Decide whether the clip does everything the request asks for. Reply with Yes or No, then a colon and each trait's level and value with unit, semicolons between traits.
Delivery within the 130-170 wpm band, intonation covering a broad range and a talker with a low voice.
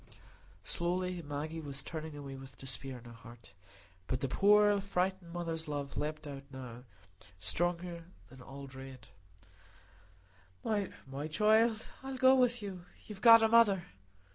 No: average, 140 wpm; wide, 6.7 semitones; medium, 165 Hz